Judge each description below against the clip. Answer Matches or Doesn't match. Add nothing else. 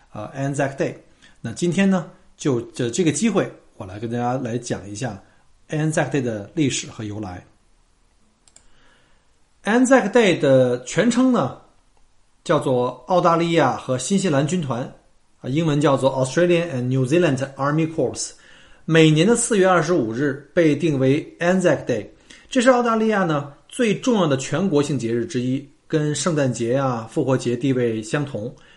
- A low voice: Doesn't match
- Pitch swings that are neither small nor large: Doesn't match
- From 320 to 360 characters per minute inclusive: Matches